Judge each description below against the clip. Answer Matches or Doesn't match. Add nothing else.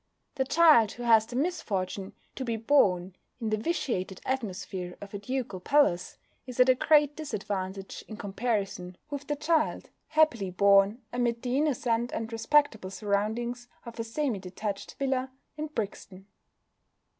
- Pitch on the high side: Matches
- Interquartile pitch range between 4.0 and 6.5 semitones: Matches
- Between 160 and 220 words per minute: Doesn't match